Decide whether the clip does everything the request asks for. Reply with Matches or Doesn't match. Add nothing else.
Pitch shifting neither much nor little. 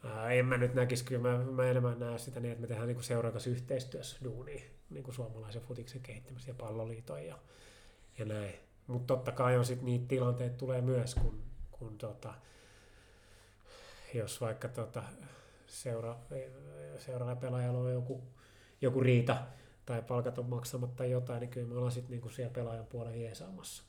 Doesn't match